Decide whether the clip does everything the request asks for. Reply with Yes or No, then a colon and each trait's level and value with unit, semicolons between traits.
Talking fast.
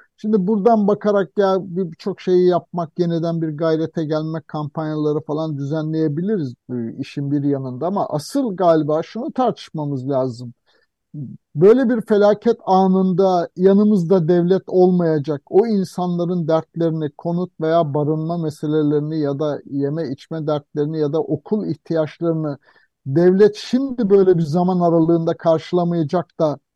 No: average, 125 wpm